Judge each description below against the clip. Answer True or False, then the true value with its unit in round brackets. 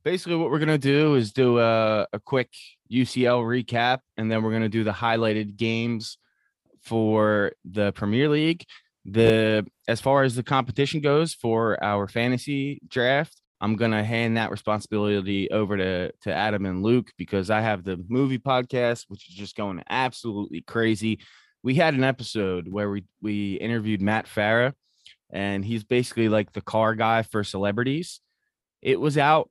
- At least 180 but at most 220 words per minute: False (170 wpm)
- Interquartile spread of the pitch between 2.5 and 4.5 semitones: True (3.4 semitones)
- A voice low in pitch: True (115 Hz)